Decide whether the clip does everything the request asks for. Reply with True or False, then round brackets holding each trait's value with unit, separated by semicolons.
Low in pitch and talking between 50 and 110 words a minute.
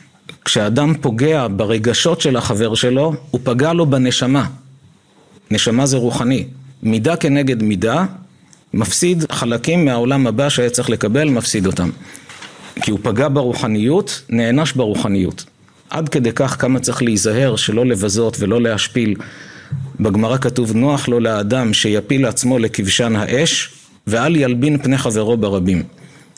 False (125 Hz; 125 wpm)